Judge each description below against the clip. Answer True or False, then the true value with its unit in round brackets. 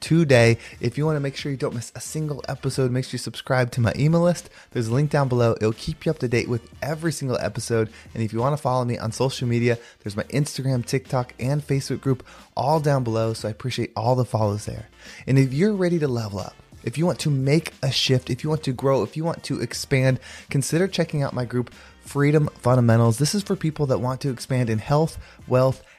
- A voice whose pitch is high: False (130 Hz)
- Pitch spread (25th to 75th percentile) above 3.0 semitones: True (3.7 semitones)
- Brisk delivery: True (240 wpm)